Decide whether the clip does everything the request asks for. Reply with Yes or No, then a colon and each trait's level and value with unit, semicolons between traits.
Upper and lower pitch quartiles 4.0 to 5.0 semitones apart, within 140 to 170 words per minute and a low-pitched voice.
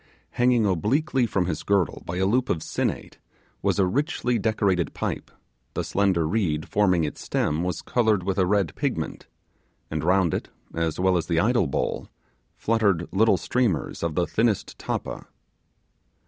Yes: average, 4.5 semitones; average, 160 wpm; very low, 95 Hz